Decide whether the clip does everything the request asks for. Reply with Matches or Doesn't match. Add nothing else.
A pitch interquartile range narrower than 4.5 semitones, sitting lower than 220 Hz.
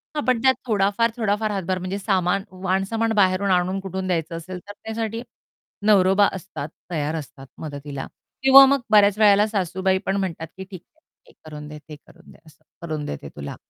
Matches